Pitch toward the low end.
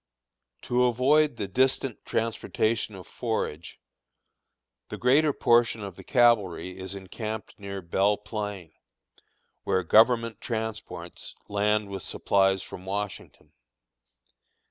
Yes: low, 105 Hz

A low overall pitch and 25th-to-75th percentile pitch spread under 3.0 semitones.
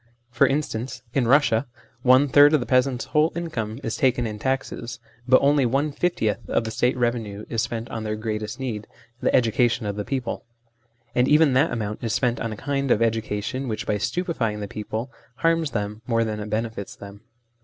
No: low, 120 Hz; average, 3.8 semitones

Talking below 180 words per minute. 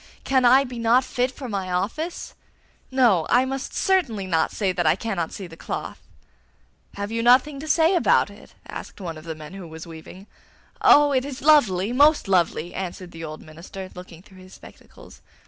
No: average, 190 wpm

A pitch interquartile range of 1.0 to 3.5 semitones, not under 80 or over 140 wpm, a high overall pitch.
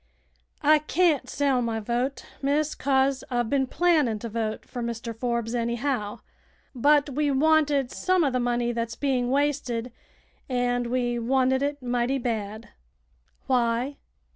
Yes: average, 3.1 semitones; slow, 135 wpm; very high, 250 Hz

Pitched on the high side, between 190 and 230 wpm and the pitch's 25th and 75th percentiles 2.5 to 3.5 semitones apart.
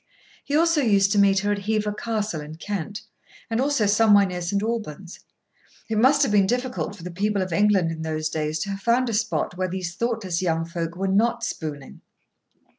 No: high, 200 Hz; average, 200 wpm; average, 4.2 semitones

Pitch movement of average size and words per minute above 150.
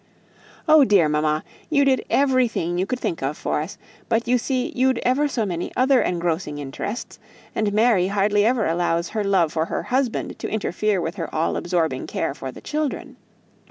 No: wide, 7.1 semitones; average, 185 wpm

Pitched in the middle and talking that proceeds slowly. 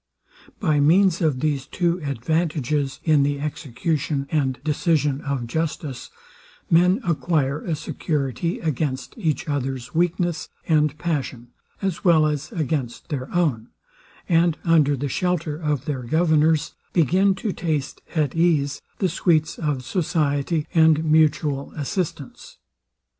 Yes: medium, 155 Hz; slow, 125 wpm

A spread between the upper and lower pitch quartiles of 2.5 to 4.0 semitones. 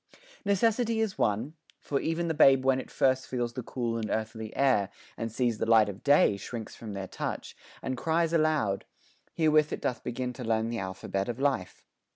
No: wide, 5.4 semitones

